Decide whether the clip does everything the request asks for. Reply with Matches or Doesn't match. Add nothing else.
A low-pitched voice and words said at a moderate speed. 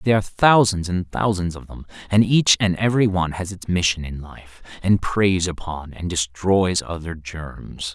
Matches